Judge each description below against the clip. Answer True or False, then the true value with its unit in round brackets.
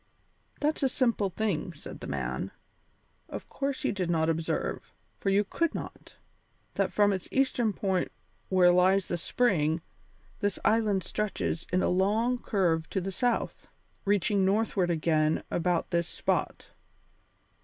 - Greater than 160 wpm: False (145 wpm)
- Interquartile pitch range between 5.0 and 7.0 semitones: False (3.8 semitones)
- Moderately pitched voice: False (195 Hz)